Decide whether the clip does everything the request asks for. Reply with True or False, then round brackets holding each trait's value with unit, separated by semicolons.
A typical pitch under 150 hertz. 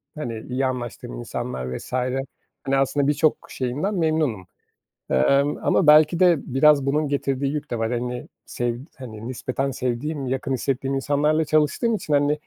True (135 Hz)